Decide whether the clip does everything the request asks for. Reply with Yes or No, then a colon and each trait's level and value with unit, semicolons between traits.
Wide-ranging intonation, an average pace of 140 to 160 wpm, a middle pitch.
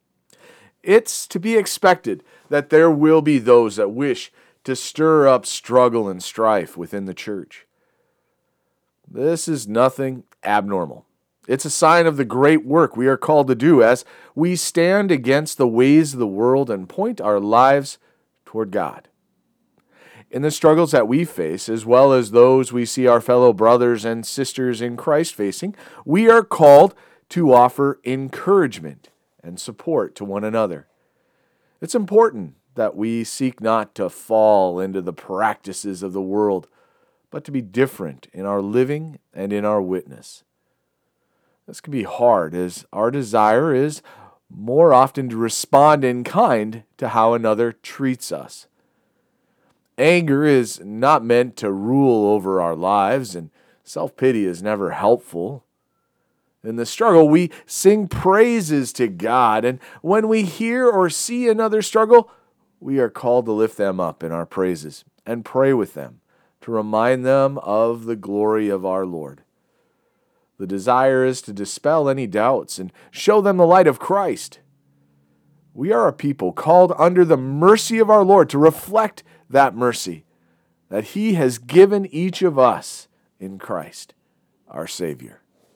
No: wide, 6.8 semitones; average, 155 wpm; low, 130 Hz